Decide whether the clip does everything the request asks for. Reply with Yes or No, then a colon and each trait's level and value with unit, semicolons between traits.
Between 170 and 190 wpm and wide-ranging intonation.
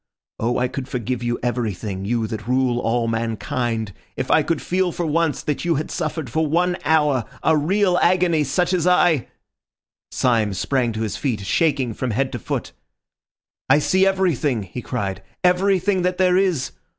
Yes: average, 175 wpm; wide, 6.8 semitones